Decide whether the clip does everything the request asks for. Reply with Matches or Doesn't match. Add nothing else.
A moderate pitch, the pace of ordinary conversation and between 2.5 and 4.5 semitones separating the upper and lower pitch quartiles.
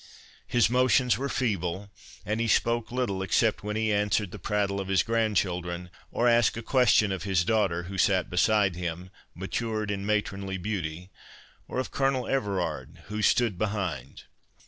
Doesn't match